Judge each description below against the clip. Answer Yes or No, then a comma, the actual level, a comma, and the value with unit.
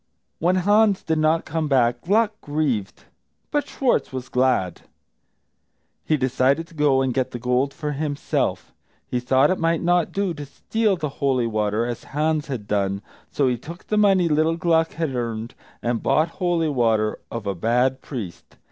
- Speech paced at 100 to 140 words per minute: No, average, 175 wpm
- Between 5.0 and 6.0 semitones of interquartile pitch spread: Yes, average, 5.3 semitones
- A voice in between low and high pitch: Yes, medium, 145 Hz